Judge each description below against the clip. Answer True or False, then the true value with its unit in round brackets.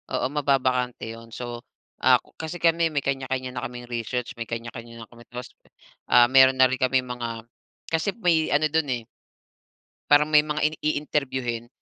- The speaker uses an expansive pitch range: False (3.8 semitones)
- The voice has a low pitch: True (130 Hz)